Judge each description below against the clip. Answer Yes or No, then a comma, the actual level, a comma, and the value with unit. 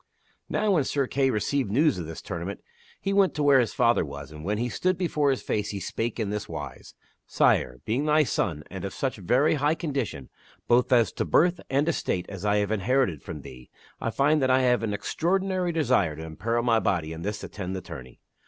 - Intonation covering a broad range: Yes, wide, 7.1 semitones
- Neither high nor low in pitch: No, low, 115 Hz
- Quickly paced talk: Yes, fast, 225 wpm